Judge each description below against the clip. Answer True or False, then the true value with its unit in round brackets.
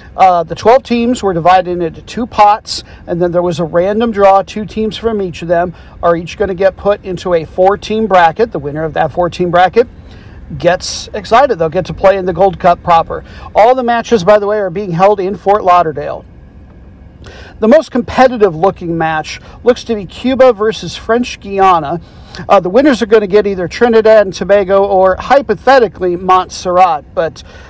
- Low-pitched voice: False (195 Hz)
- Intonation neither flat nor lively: True (4.1 semitones)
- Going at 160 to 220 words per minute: True (195 wpm)